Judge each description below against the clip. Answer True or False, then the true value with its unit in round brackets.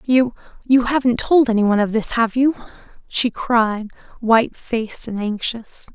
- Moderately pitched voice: False (235 Hz)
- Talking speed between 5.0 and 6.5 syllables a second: False (4.5 syllables/s)